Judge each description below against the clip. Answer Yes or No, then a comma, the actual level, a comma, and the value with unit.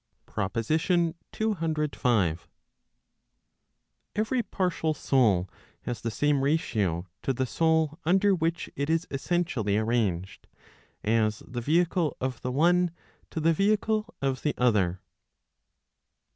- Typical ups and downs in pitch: No, wide, 7.0 semitones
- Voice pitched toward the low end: No, medium, 145 Hz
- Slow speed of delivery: Yes, slow, 110 wpm